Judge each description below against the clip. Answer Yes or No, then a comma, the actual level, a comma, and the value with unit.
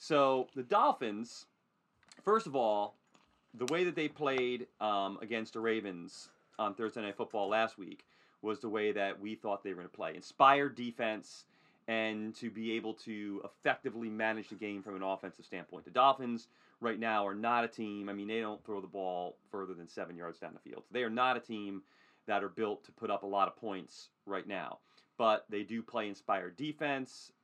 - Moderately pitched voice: No, low, 110 Hz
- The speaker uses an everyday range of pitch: Yes, average, 3.1 semitones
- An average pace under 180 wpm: No, fast, 205 wpm